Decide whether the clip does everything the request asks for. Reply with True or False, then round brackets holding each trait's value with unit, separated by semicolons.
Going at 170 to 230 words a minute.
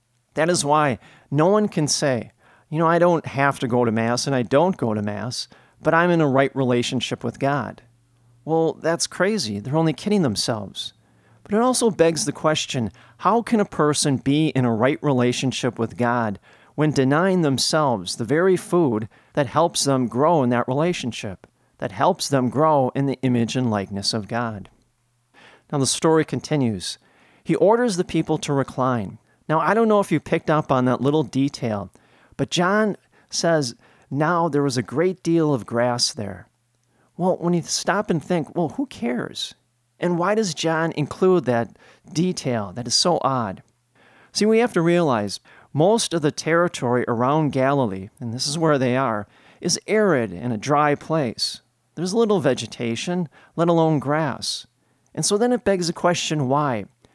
True (175 wpm)